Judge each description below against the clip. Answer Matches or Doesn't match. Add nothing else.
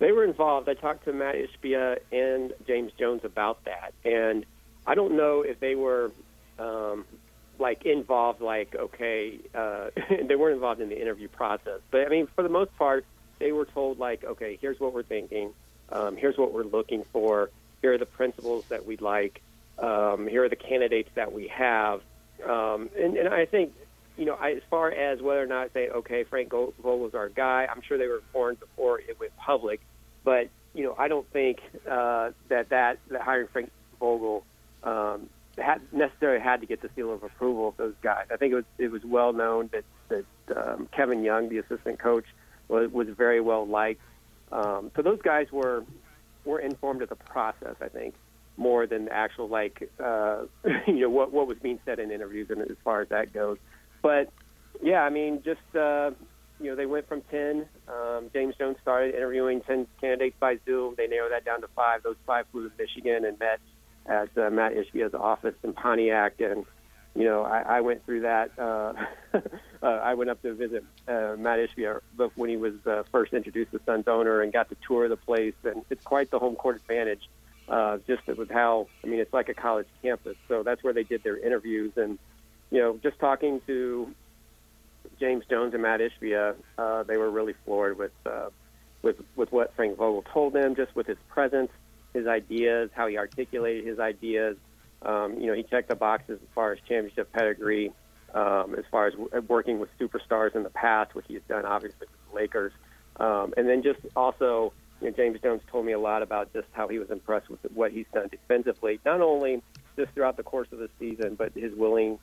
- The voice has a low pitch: Matches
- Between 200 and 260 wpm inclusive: Matches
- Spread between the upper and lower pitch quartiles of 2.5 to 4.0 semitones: Matches